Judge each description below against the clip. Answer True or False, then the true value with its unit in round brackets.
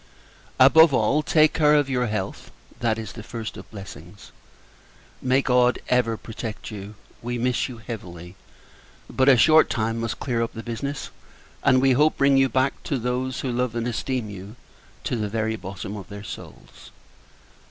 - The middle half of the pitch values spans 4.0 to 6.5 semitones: False (3.3 semitones)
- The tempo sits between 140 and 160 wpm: False (175 wpm)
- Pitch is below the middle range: True (120 Hz)